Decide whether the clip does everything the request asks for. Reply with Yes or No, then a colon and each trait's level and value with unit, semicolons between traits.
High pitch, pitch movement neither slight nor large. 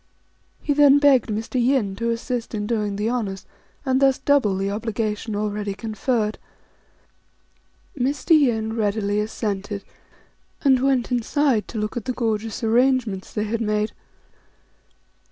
Yes: high, 225 Hz; average, 3.4 semitones